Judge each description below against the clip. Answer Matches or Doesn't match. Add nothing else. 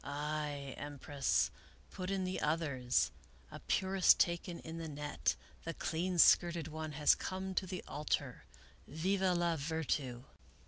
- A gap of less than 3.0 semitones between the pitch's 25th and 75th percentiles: Doesn't match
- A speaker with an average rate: Matches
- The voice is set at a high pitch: Doesn't match